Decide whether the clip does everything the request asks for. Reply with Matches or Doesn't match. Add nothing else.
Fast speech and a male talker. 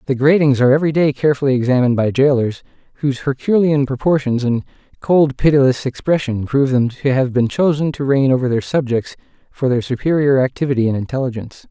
Doesn't match